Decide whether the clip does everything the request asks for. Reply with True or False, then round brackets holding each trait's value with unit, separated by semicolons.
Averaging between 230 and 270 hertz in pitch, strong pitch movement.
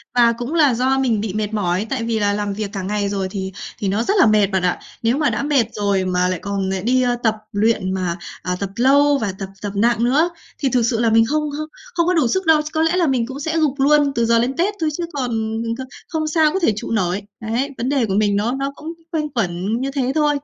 True (235 Hz; 5.9 semitones)